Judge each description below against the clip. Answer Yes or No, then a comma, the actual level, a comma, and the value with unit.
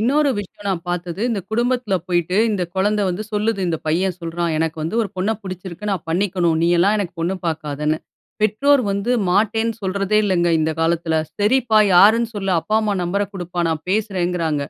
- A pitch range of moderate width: Yes, average, 3.7 semitones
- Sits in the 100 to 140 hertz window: No, high, 190 Hz